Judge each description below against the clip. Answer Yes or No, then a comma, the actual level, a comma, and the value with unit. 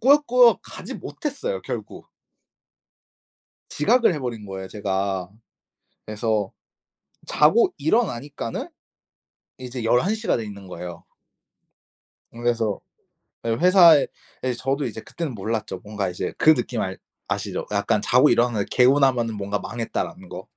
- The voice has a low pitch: Yes, low, 120 Hz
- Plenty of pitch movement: Yes, wide, 6.3 semitones